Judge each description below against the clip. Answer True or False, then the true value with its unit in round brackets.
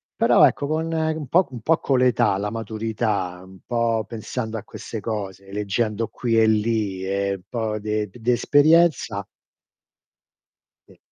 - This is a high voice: False (110 Hz)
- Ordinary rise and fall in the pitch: True (3.3 semitones)